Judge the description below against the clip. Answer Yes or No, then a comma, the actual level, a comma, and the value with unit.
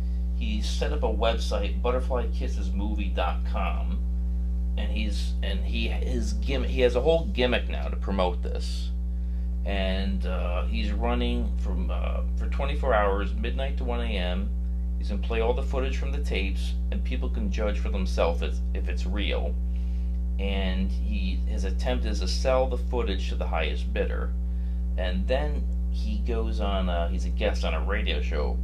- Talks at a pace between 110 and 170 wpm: Yes, average, 165 wpm